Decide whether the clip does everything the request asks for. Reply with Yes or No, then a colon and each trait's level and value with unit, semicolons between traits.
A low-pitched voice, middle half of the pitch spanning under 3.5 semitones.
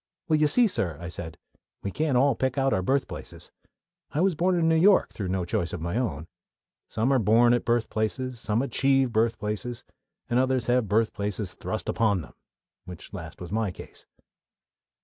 No: low, 115 Hz; wide, 5.4 semitones